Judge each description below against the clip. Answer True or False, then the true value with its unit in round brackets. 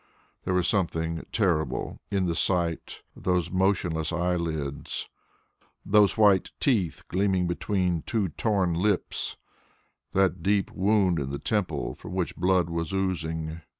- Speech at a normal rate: False (130 wpm)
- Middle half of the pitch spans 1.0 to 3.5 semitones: True (2.7 semitones)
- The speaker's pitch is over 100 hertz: False (90 Hz)